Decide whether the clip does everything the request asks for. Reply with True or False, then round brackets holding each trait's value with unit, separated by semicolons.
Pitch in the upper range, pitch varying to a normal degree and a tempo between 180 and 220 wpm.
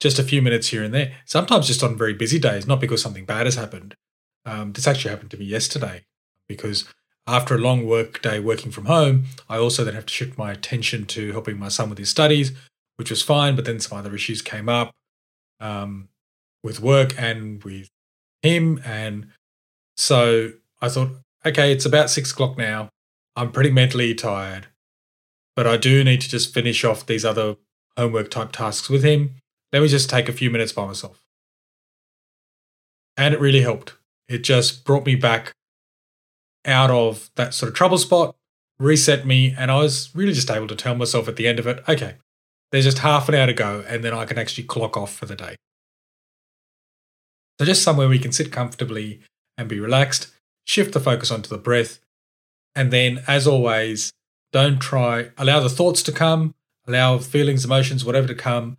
False (120 Hz; 3.6 semitones; 190 wpm)